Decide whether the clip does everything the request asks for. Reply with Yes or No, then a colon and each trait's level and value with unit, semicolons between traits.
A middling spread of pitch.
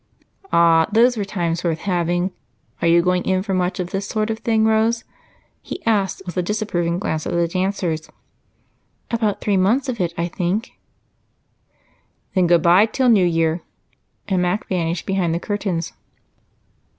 Yes: average, 3.6 semitones